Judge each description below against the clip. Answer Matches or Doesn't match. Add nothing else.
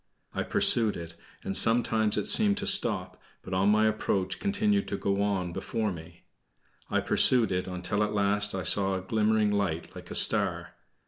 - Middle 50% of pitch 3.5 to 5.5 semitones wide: Doesn't match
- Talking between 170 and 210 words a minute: Matches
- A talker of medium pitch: Doesn't match